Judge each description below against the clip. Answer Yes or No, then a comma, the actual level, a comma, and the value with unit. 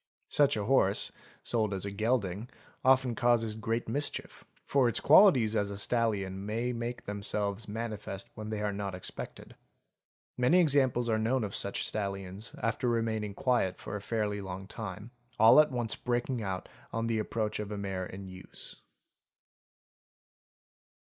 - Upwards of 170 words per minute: No, average, 155 wpm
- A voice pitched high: No, low, 110 Hz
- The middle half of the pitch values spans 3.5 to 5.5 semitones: No, average, 3.1 semitones